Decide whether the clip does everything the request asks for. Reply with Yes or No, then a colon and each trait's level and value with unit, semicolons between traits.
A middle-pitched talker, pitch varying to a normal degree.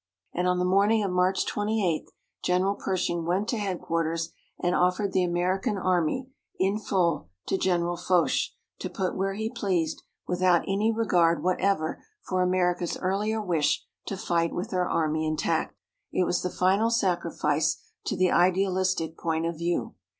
No: medium, 180 Hz; narrow, 2.2 semitones